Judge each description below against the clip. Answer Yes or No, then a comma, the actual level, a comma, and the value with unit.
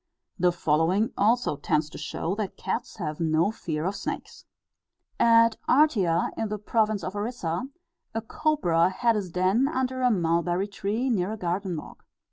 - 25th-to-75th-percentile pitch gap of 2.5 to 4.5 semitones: No, average, 5.1 semitones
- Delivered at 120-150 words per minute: No, average, 160 wpm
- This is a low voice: No, high, 195 Hz